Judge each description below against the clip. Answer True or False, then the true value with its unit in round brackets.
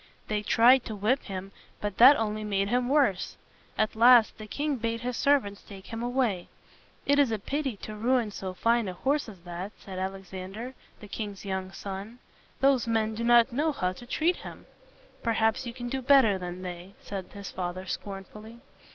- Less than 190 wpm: False (200 wpm)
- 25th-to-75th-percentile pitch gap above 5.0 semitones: False (4.1 semitones)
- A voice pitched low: False (220 Hz)